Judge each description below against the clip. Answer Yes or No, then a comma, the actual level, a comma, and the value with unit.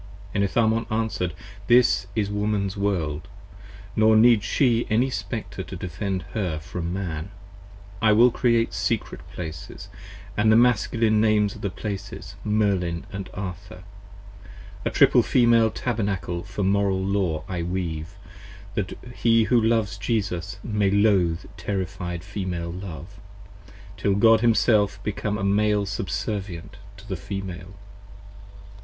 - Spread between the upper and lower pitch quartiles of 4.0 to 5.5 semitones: No, average, 3.1 semitones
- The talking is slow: Yes, slow, 125 wpm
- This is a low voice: Yes, low, 100 Hz